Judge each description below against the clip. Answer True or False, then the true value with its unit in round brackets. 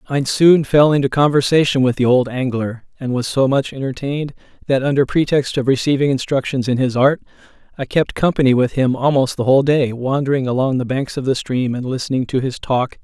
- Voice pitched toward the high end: False (135 Hz)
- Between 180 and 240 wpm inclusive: True (205 wpm)